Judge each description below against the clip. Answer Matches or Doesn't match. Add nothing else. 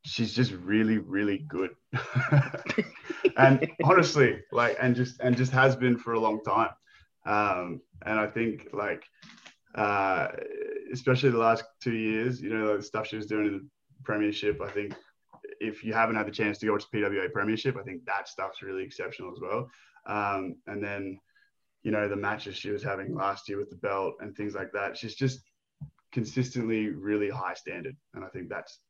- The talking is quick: Doesn't match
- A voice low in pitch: Matches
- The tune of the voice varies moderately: Matches